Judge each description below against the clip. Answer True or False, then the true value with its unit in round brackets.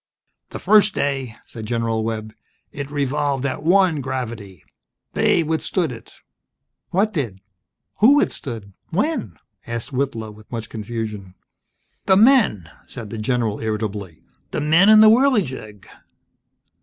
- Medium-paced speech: False (130 wpm)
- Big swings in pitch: True (7.2 semitones)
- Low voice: True (125 Hz)